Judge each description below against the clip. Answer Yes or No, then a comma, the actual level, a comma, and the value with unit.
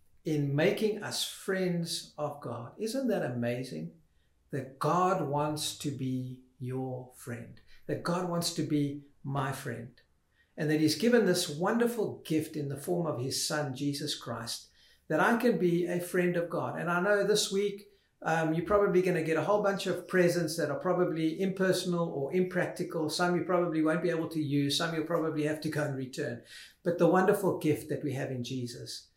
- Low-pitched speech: No, medium, 160 Hz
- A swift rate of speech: No, average, 190 wpm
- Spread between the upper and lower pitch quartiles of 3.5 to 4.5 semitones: Yes, average, 4.2 semitones